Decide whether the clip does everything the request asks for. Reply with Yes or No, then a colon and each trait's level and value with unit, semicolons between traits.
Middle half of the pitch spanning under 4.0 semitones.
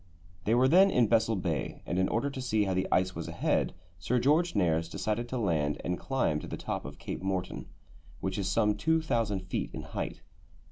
No: average, 5.1 semitones